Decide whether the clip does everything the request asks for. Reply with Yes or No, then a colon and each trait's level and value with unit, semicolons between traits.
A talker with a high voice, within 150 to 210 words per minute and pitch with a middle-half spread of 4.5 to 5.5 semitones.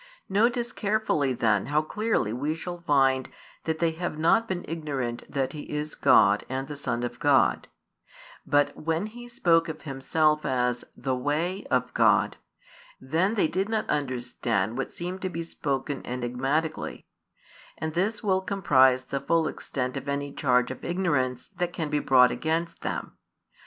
No: medium, 150 Hz; average, 160 wpm; average, 4.9 semitones